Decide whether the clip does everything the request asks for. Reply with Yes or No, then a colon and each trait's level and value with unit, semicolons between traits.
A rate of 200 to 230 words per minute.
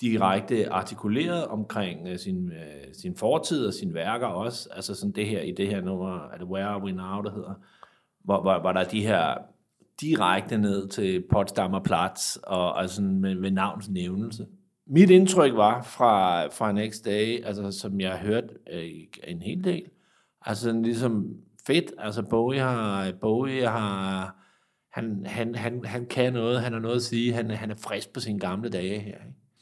No: average, 175 wpm